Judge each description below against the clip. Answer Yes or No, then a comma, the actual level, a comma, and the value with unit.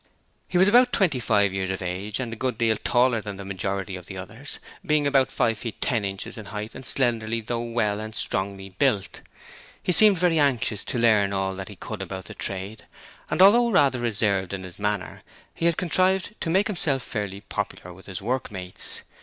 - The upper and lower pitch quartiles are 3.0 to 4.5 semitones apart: No, wide, 5.6 semitones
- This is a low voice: Yes, low, 110 Hz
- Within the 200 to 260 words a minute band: Yes, fast, 205 wpm